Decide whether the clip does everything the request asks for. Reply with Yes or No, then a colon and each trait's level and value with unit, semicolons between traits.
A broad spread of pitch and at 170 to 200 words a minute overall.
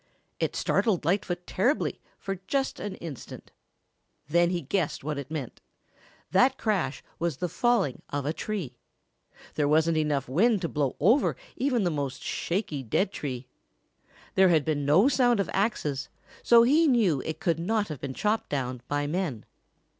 No: wide, 6.5 semitones; average, 160 wpm